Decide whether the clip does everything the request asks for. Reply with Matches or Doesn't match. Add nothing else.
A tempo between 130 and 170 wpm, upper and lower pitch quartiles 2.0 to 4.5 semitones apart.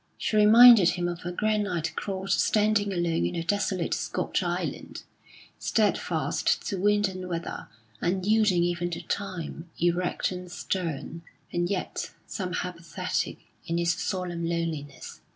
Matches